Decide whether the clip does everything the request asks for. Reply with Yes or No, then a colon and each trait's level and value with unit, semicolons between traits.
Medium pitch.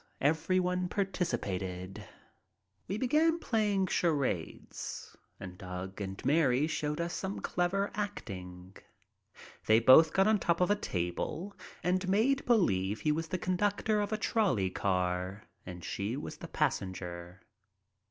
Yes: medium, 160 Hz